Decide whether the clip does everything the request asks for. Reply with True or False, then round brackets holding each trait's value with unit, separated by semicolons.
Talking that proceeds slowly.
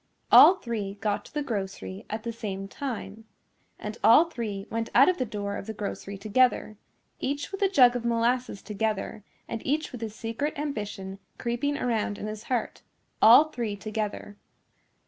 False (170 wpm)